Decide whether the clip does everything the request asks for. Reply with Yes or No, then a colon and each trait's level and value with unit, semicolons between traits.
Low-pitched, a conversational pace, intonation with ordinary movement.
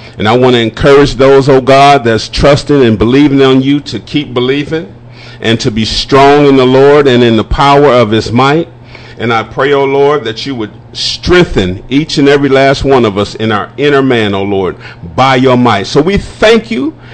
No: low, 130 Hz; fast, 220 wpm; average, 3.6 semitones